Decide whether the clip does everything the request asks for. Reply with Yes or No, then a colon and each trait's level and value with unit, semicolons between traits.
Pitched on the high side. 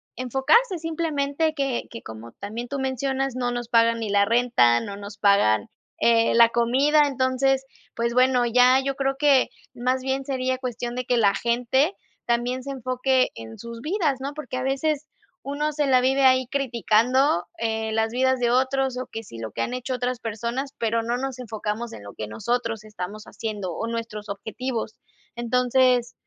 Yes: very high, 250 Hz